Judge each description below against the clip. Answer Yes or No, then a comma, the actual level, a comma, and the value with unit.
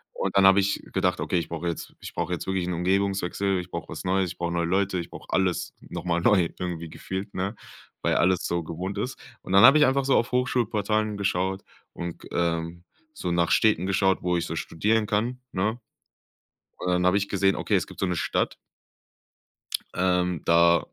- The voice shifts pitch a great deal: No, narrow, 2.5 semitones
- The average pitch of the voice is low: Yes, very low, 95 Hz